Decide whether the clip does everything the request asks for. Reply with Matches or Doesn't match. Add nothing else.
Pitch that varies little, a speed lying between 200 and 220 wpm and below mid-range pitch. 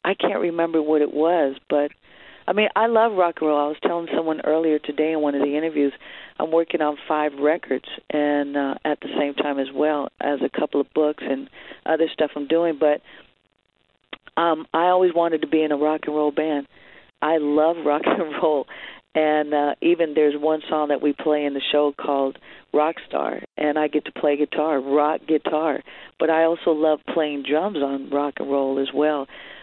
Doesn't match